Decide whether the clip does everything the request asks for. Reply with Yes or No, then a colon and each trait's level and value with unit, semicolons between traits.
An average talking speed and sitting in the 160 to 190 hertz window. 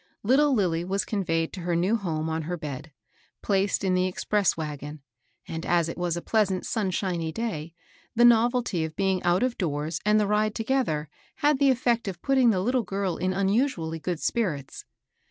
Yes: average, 185 wpm; medium, 185 Hz